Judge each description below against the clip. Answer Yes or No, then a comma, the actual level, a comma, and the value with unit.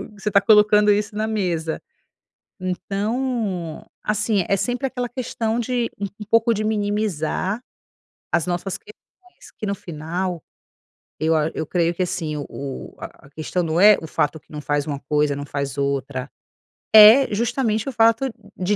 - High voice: Yes, high, 200 Hz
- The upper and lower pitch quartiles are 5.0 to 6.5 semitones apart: Yes, wide, 5.5 semitones